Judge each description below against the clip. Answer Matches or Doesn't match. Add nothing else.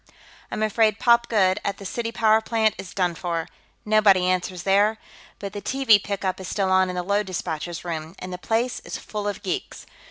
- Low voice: Doesn't match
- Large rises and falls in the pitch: Doesn't match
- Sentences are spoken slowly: Doesn't match